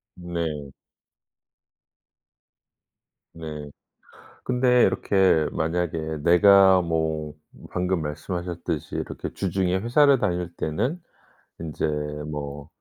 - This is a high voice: No, very low, 85 Hz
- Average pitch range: Yes, average, 3.6 semitones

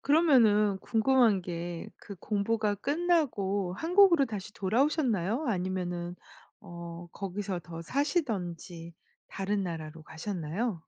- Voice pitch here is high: Yes, high, 200 Hz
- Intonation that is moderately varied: No, wide, 5.9 semitones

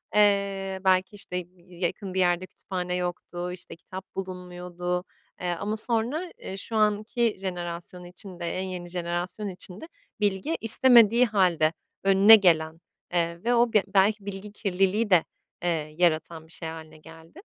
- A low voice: No, medium, 185 Hz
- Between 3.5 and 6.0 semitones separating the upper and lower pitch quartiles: No, average, 2.8 semitones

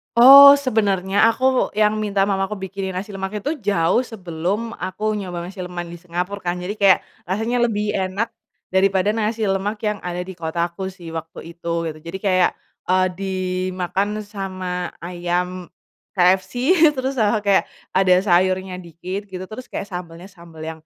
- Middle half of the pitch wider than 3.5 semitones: No, average, 2.7 semitones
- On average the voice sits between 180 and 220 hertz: Yes, high, 190 Hz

